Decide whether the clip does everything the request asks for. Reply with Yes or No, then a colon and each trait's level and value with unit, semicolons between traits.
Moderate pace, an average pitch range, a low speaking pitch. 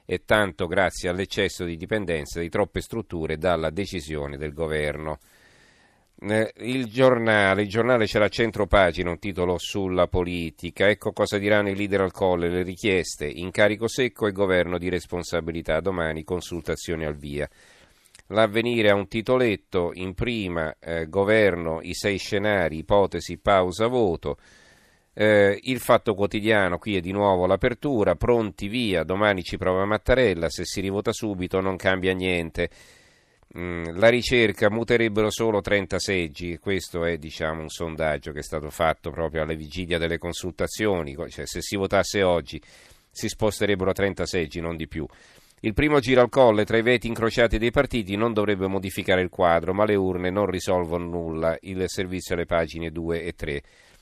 Yes: average, 155 wpm; average, 3.8 semitones; very low, 95 Hz